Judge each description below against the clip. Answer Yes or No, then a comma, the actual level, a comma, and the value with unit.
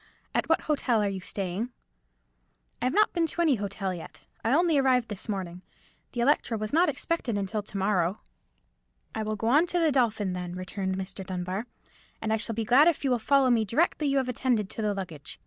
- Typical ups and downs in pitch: No, wide, 5.8 semitones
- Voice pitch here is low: No, high, 220 Hz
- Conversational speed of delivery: No, fast, 215 wpm